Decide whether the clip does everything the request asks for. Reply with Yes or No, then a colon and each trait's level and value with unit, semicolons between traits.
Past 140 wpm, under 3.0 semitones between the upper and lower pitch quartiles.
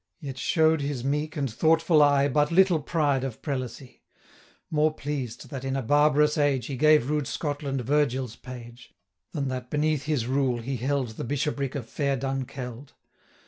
Yes: average, 170 wpm; narrow, 2.6 semitones